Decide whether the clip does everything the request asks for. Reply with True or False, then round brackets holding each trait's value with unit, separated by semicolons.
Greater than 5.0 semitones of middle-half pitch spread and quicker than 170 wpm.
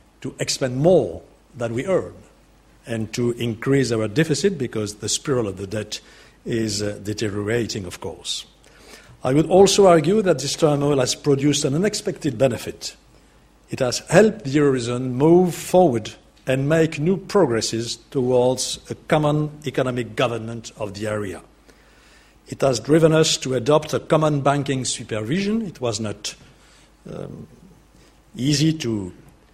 False (5.6 semitones; 140 wpm)